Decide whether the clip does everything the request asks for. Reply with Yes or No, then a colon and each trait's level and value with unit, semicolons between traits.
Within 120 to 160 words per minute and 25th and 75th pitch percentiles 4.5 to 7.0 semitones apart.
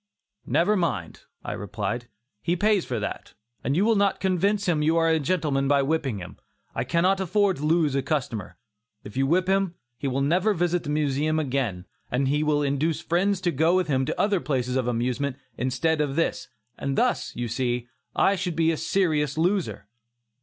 No: average, 195 wpm; average, 4.9 semitones